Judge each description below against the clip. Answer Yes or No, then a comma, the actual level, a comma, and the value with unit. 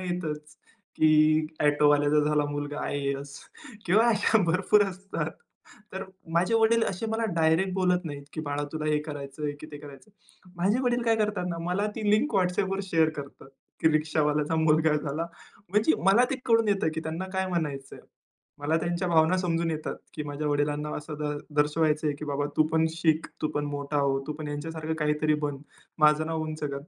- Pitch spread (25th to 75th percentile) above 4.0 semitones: No, average, 3.7 semitones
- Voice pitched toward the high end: No, medium, 155 Hz